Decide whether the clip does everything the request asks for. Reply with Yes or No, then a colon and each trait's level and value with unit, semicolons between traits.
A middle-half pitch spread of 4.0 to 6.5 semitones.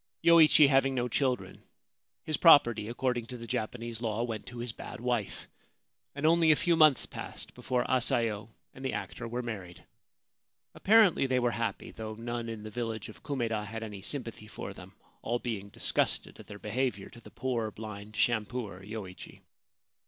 No: average, 3.1 semitones